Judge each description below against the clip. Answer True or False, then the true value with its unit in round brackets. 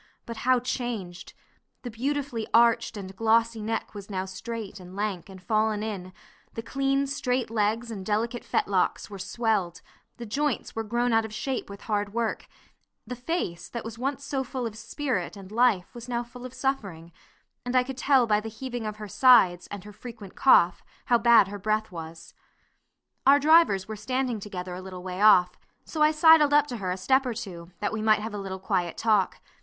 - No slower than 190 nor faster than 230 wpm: True (200 wpm)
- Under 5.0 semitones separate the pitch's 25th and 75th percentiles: True (4.1 semitones)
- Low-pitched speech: False (220 Hz)